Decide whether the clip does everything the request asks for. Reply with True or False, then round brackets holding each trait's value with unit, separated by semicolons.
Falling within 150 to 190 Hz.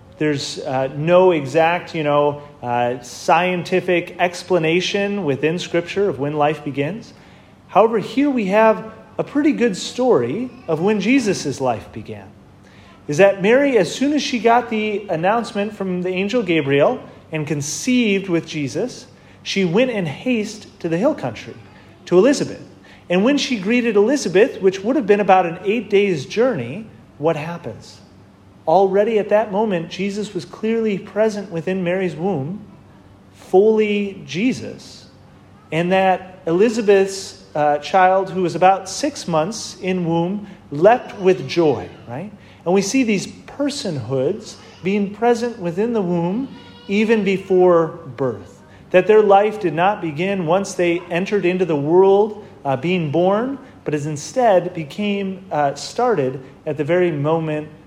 True (185 Hz)